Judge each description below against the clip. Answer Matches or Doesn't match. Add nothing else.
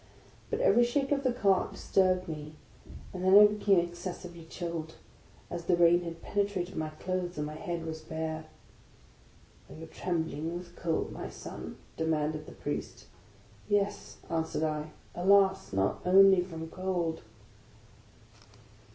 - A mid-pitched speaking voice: Matches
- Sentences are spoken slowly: Doesn't match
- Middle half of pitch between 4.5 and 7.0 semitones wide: Doesn't match